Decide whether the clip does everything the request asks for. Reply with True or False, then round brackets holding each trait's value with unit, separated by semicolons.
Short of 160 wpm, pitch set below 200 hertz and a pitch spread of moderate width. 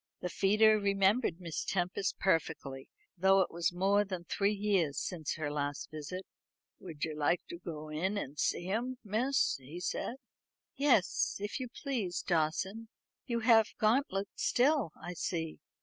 True (150 wpm; 190 Hz; 4.6 semitones)